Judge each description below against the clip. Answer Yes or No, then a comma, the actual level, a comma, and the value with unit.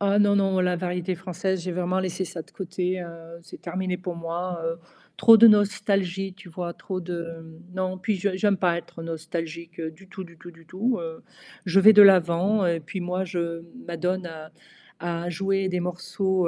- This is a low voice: No, medium, 180 Hz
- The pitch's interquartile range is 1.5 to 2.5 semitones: Yes, narrow, 2.1 semitones